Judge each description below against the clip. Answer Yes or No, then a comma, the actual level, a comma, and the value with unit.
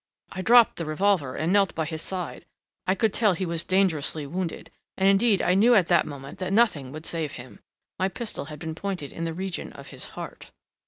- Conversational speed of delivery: No, fast, 215 wpm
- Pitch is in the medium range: Yes, medium, 180 Hz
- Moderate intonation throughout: Yes, average, 3.8 semitones